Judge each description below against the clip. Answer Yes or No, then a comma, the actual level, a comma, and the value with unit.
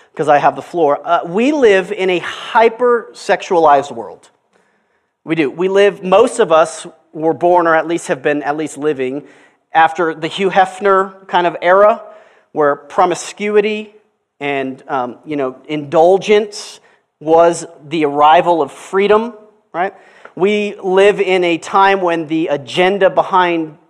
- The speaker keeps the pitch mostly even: No, average, 3.9 semitones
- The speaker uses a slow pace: No, average, 145 wpm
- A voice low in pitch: No, medium, 175 Hz